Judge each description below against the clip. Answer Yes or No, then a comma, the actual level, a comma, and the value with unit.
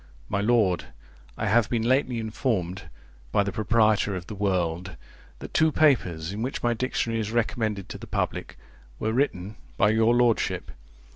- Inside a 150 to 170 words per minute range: Yes, average, 160 wpm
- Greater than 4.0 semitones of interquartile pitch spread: No, average, 3.3 semitones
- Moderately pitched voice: No, low, 110 Hz